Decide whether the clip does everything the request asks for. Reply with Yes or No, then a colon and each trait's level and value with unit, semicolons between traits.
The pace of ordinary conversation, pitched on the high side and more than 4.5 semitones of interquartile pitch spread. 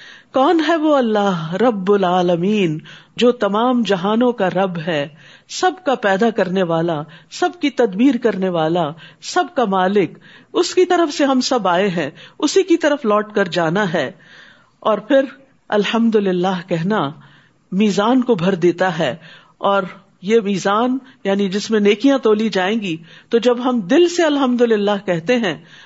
Yes: average, 160 wpm; high, 205 Hz; wide, 5.5 semitones